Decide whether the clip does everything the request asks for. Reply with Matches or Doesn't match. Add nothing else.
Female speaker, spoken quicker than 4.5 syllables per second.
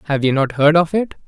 Doesn't match